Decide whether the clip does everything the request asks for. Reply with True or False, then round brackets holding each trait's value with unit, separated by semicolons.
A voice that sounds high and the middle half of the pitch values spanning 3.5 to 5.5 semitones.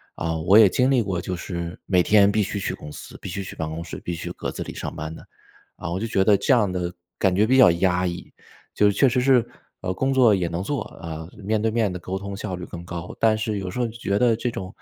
False (95 Hz; 4.0 semitones)